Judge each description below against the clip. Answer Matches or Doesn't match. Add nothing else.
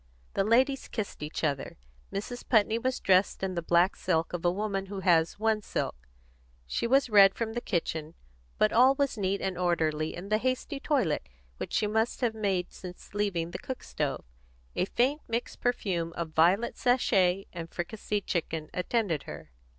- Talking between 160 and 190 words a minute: Matches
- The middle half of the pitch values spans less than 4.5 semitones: Doesn't match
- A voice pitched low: Doesn't match